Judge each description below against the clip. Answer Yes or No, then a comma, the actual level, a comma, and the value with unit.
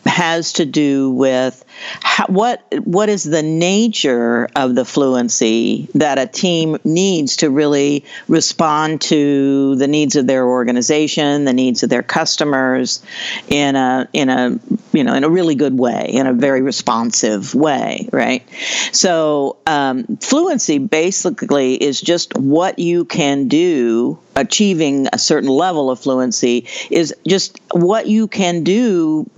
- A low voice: No, medium, 150 Hz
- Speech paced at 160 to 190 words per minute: No, average, 145 wpm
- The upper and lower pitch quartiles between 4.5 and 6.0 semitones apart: Yes, wide, 5.4 semitones